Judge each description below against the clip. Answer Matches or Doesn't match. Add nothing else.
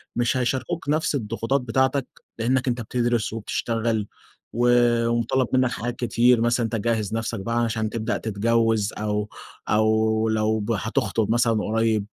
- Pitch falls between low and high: Doesn't match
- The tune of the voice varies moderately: Doesn't match